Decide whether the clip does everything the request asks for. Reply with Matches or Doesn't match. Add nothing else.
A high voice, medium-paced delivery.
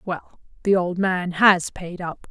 Doesn't match